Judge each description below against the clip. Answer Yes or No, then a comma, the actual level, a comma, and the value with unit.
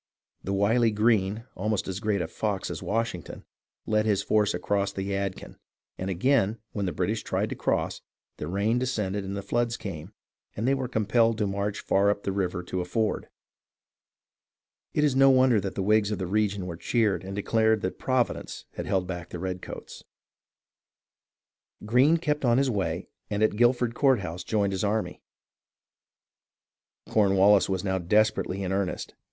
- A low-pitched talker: Yes, low, 105 Hz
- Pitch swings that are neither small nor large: Yes, average, 3.0 semitones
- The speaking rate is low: No, average, 170 wpm